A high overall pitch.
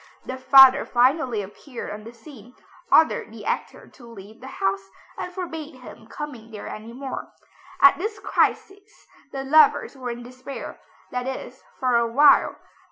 Yes: very high, 255 Hz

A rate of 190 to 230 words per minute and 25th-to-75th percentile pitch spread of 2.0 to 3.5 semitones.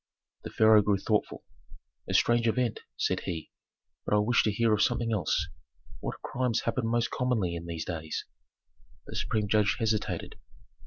No: average, 160 wpm; average, 3.1 semitones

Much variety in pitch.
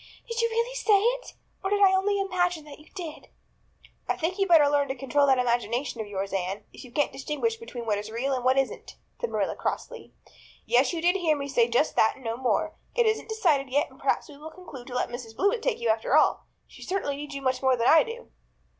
Yes: wide, 7.6 semitones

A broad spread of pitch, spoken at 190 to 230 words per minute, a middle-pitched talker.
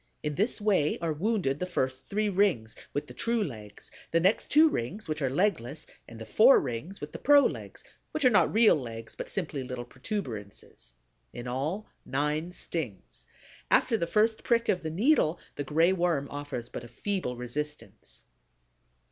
No: wide, 8.4 semitones; average, 175 wpm; medium, 155 Hz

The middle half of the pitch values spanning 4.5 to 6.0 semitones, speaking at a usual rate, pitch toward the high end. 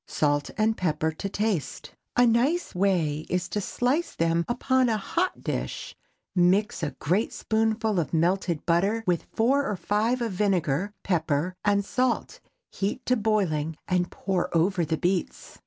Yes: average, 4.8 semitones; average, 155 wpm; high, 195 Hz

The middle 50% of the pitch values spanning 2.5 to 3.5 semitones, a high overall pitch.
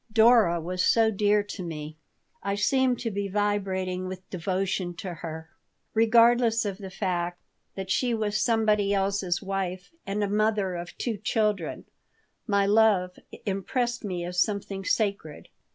Yes: average, 2.8 semitones; high, 200 Hz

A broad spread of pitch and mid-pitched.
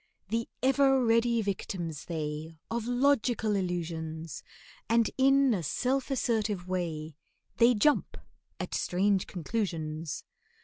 No: wide, 6.5 semitones; high, 205 Hz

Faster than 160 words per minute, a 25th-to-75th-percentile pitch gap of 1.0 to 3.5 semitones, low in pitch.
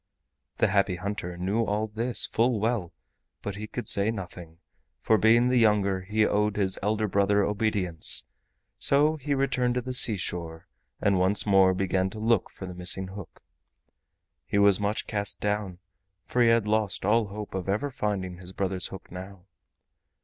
Yes: average, 170 wpm; average, 2.7 semitones; low, 100 Hz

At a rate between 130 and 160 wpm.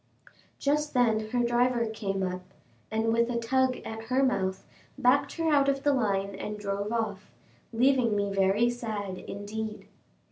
Yes: average, 155 wpm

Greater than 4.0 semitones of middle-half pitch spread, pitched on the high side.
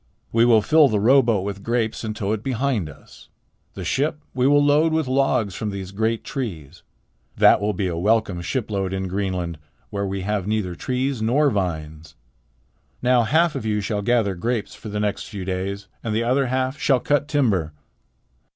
No: average, 4.8 semitones; low, 110 Hz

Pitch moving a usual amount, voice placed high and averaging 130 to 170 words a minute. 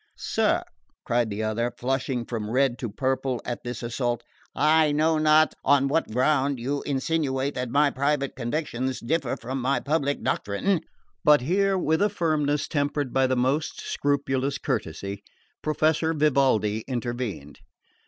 No: average, 3.7 semitones; low, 135 Hz; average, 145 wpm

